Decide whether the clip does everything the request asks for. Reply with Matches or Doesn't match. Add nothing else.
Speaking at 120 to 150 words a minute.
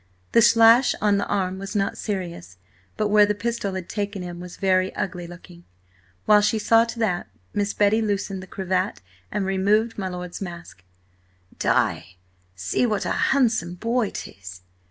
Doesn't match